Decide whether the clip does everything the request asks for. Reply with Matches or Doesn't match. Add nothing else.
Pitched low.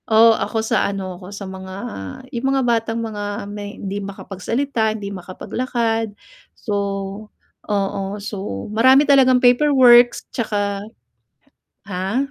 Doesn't match